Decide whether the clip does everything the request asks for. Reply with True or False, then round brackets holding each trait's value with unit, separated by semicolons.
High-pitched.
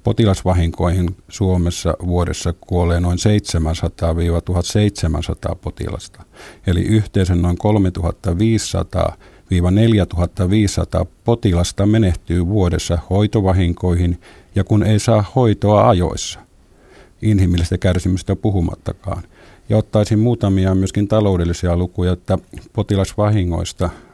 False (95 Hz)